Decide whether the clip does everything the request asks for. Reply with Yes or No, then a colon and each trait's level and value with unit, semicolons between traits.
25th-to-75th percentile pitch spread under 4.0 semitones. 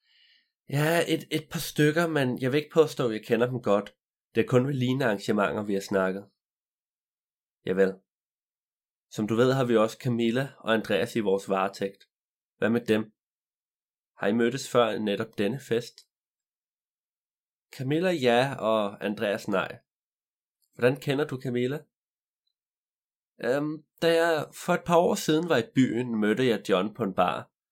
No: wide, 5.6 semitones